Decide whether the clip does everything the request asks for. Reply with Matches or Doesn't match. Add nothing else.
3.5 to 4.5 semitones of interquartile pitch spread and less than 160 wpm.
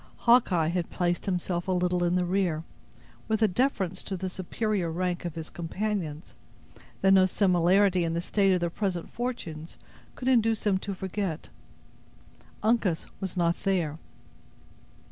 Doesn't match